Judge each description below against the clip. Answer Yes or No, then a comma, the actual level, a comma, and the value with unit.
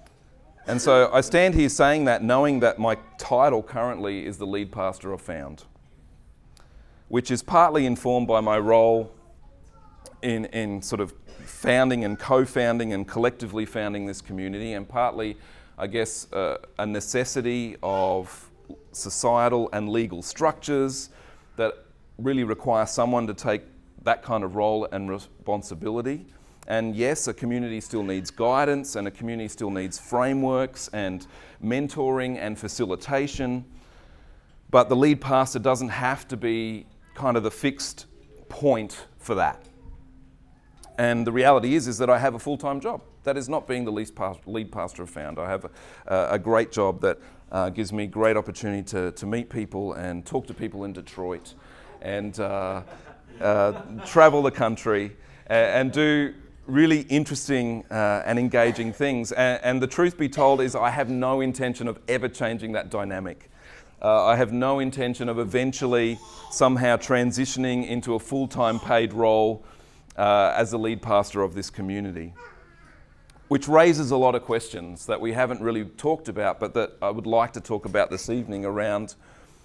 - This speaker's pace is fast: No, average, 160 wpm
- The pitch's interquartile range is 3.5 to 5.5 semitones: Yes, average, 3.9 semitones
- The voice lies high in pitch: No, low, 115 Hz